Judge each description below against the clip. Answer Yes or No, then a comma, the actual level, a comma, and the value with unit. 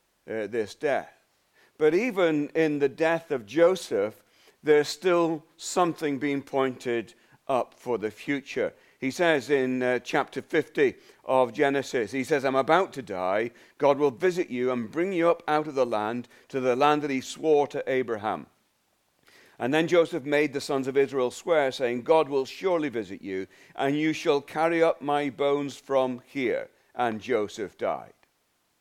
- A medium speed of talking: Yes, average, 165 wpm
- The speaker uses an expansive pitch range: No, average, 4.0 semitones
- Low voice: No, medium, 145 Hz